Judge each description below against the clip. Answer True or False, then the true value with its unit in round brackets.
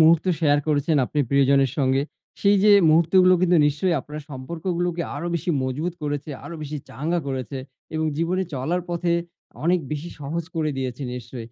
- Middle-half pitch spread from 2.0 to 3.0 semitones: False (3.7 semitones)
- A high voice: False (155 Hz)